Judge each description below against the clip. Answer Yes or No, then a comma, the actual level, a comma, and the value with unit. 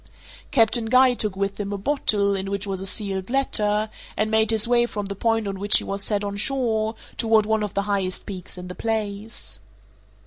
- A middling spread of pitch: No, narrow, 2.1 semitones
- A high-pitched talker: Yes, high, 210 Hz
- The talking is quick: Yes, fast, 210 wpm